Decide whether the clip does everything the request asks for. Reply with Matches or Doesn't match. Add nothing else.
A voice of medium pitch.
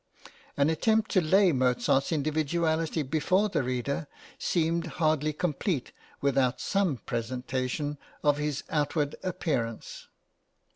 Matches